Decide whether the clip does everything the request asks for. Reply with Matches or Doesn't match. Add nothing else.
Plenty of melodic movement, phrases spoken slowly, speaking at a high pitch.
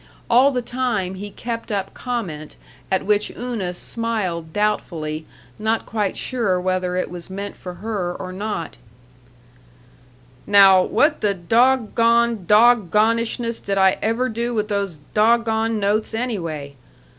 Doesn't match